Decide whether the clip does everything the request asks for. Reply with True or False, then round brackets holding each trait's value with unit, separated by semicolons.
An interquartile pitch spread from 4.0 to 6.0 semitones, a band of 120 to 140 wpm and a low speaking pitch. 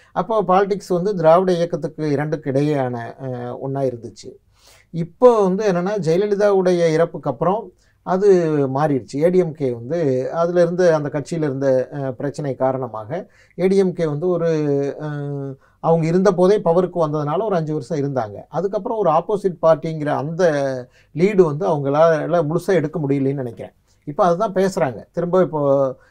False (4.7 semitones; 125 wpm; 160 Hz)